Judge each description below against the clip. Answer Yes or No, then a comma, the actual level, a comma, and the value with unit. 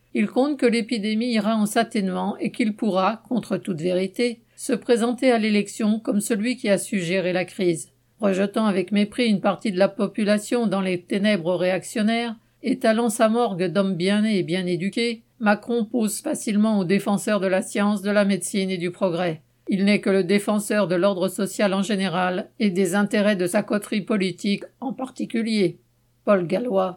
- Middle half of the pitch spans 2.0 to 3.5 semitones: Yes, average, 2.9 semitones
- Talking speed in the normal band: Yes, average, 180 wpm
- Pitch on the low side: No, high, 205 Hz